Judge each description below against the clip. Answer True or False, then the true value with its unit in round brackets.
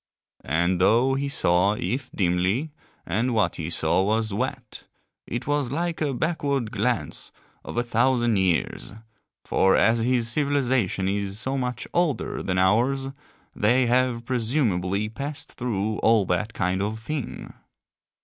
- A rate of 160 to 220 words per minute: False (140 wpm)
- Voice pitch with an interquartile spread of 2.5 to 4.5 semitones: False (5.0 semitones)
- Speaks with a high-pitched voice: False (115 Hz)